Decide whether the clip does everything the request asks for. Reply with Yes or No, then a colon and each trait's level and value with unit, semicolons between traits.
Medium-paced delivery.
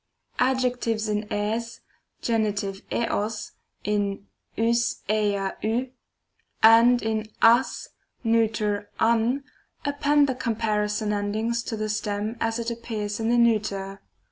No: slow, 115 wpm